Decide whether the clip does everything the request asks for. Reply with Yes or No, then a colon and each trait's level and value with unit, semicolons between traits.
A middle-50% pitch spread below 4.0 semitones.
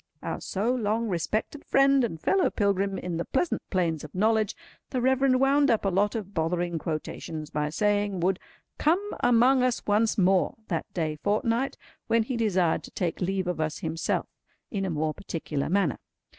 No: wide, 5.5 semitones